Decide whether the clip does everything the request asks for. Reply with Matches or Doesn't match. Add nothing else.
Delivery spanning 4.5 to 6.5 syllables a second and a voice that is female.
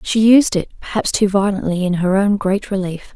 Matches